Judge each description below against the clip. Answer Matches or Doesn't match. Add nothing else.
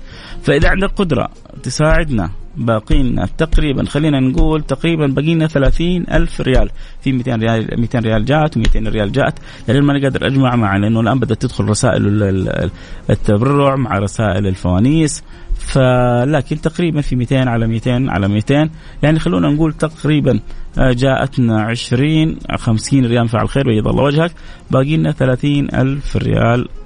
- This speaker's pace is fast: Matches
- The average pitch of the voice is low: Matches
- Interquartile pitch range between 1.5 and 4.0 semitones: Doesn't match